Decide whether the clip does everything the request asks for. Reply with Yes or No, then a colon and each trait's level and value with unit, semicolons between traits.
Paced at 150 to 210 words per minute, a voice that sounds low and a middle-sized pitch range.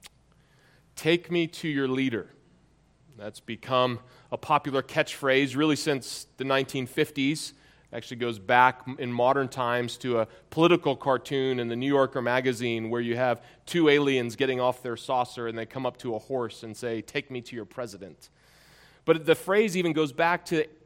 Yes: average, 175 wpm; low, 130 Hz; average, 3.5 semitones